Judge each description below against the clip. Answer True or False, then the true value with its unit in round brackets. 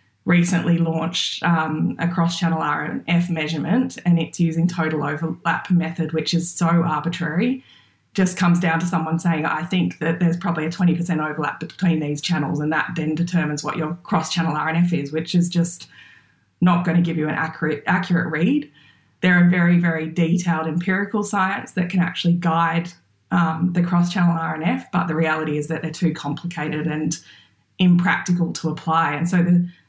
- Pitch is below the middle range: False (170 Hz)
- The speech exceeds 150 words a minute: True (170 wpm)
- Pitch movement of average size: False (1.7 semitones)